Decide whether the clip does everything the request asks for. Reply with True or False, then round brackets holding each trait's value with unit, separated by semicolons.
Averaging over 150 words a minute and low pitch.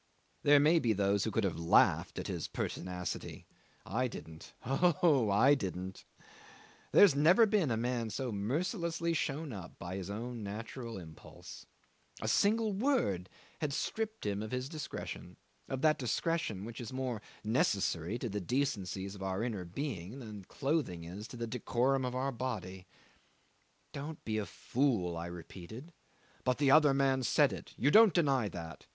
True (165 wpm; 120 Hz)